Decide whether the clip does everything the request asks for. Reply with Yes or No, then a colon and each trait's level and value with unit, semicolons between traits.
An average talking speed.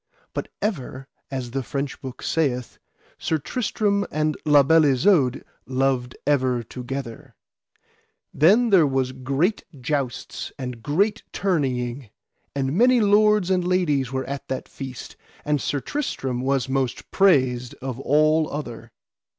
No: slow, 130 wpm